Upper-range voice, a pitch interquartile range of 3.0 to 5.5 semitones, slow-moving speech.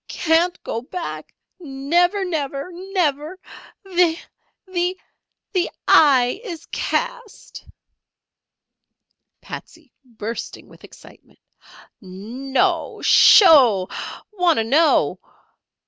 Yes: very high, 325 Hz; average, 5.2 semitones; slow, 75 wpm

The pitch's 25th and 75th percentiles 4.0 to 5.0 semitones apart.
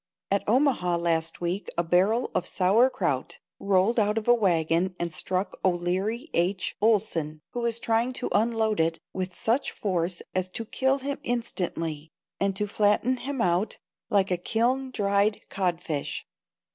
Yes: average, 4.5 semitones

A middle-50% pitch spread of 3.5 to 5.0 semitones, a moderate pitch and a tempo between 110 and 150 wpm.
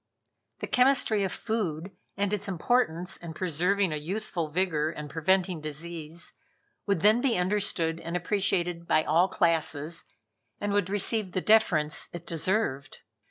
Yes: average, 3.9 semitones; medium, 175 Hz; average, 140 wpm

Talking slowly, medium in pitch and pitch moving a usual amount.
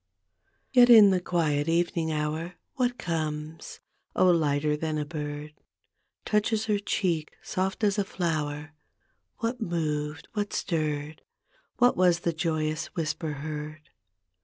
Yes: slow, 125 wpm; medium, 160 Hz; average, 3.6 semitones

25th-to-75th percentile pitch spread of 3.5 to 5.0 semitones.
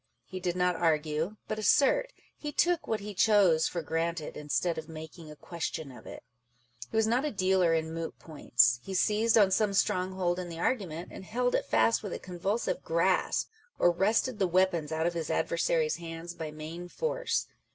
Yes: average, 4.5 semitones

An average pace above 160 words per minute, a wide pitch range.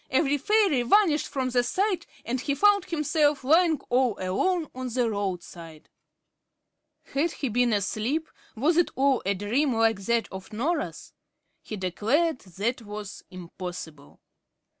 No: slow, 135 wpm; wide, 6.8 semitones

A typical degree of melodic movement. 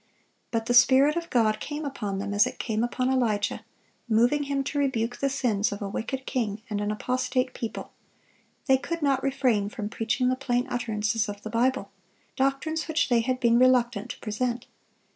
Yes: average, 3.6 semitones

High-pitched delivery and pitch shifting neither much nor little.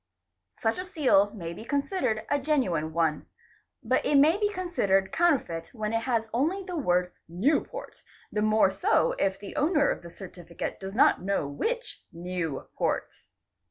No: high, 220 Hz; wide, 8.8 semitones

